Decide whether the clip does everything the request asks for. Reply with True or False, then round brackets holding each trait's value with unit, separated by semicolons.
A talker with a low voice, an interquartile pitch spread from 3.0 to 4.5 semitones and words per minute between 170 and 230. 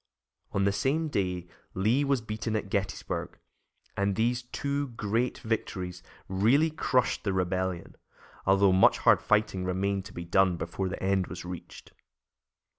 False (100 Hz; 3.8 semitones; 145 wpm)